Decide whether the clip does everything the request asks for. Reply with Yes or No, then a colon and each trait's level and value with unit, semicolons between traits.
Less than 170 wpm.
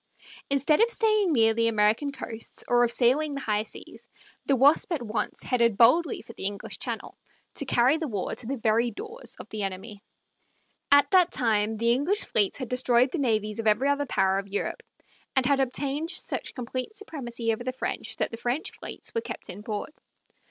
No: average, 195 wpm